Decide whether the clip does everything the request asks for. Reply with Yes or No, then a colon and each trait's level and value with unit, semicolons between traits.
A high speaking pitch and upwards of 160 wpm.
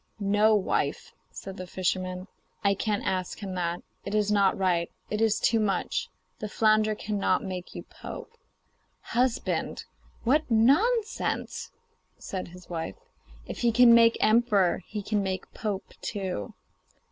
No: high, 205 Hz; average, 140 wpm